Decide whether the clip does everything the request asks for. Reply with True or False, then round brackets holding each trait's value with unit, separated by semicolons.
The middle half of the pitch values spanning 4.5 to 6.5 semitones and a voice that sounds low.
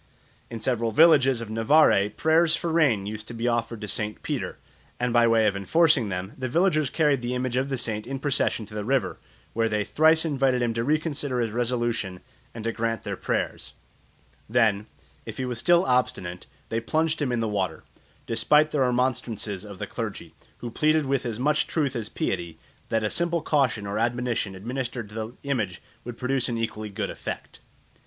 False (4.0 semitones; 120 Hz)